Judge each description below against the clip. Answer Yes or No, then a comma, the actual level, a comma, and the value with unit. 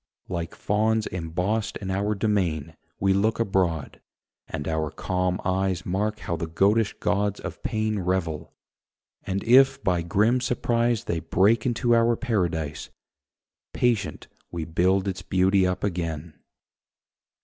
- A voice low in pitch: Yes, very low, 95 Hz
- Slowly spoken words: Yes, slow, 130 wpm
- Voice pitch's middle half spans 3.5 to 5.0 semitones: Yes, average, 4.0 semitones